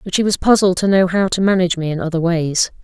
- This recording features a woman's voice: Yes, female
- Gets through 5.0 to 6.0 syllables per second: No, 6.4 syllables/s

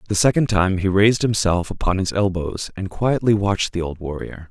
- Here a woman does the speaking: No, male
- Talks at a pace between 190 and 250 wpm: Yes, average, 200 wpm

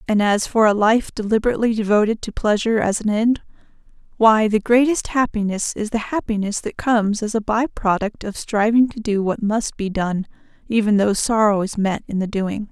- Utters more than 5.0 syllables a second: Yes, 5.3 syllables/s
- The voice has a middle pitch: No, high, 215 Hz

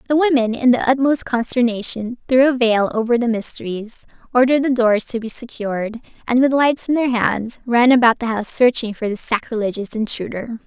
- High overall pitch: Yes, high, 235 Hz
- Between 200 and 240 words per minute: No, average, 185 wpm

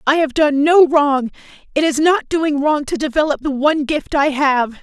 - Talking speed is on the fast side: Yes, fast, 210 wpm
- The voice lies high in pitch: Yes, very high, 290 Hz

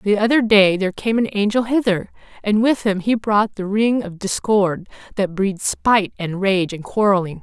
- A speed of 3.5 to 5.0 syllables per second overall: Yes, 4.8 syllables/s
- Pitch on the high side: Yes, high, 205 Hz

